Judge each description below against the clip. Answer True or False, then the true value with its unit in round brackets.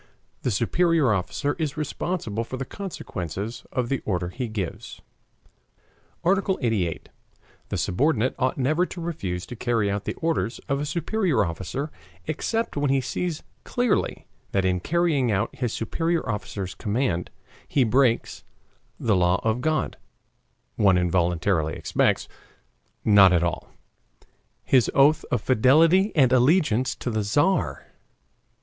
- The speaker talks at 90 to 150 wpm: True (135 wpm)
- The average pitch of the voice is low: True (125 Hz)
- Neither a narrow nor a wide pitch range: False (7.6 semitones)